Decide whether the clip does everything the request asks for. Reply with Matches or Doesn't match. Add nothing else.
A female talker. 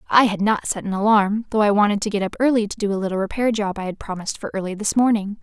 Matches